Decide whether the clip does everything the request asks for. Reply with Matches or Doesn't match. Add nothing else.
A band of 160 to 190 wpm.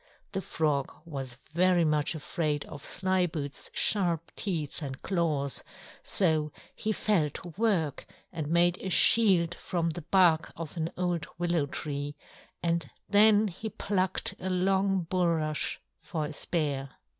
Doesn't match